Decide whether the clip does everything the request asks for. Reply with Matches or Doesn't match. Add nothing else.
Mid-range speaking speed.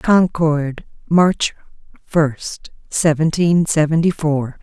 Doesn't match